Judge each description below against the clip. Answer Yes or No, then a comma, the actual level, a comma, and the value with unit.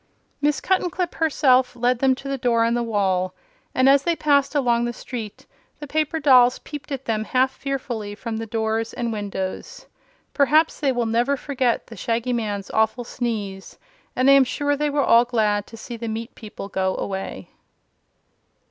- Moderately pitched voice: No, high, 245 Hz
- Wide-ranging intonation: No, average, 3.8 semitones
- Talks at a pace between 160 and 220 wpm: Yes, average, 180 wpm